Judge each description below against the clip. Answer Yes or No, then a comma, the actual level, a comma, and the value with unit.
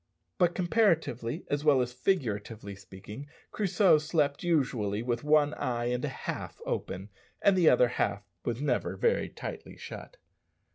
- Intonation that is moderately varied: No, wide, 6.3 semitones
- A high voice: No, medium, 140 Hz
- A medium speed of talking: Yes, average, 145 wpm